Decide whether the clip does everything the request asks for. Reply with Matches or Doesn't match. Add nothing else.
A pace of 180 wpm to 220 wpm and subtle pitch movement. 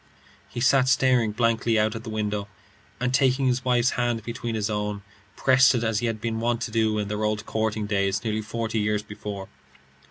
Matches